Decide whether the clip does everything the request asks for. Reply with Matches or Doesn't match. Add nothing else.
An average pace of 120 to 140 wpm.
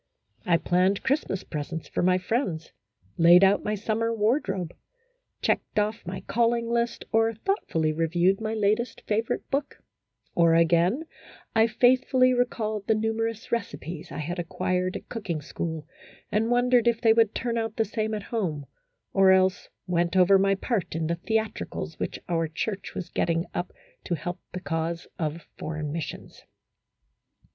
Doesn't match